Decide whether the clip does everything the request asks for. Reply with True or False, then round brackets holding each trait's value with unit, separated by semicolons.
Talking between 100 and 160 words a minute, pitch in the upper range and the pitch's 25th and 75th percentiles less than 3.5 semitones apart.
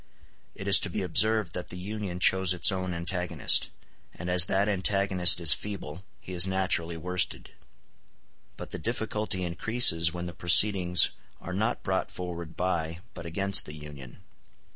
False (155 wpm; 90 Hz; 2.4 semitones)